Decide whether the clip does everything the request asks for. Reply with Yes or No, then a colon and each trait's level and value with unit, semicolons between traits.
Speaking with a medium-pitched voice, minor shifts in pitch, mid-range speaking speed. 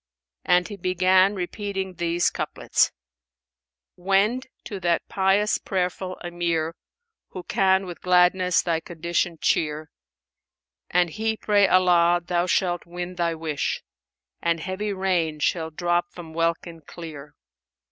No: medium, 180 Hz; narrow, 2.0 semitones; slow, 125 wpm